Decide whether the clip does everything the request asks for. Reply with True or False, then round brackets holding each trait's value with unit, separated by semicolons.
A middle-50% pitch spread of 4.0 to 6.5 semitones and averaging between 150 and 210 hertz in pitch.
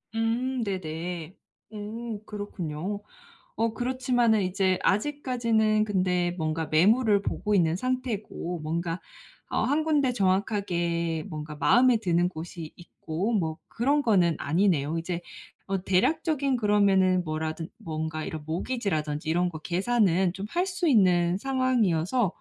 True (5.6 semitones; 190 Hz)